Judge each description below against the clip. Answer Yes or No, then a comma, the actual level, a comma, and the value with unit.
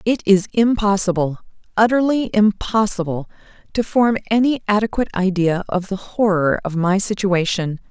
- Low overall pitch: No, high, 200 Hz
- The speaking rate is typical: No, slow, 105 wpm